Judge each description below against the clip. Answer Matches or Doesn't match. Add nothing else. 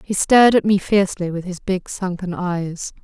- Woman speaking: Matches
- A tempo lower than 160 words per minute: Doesn't match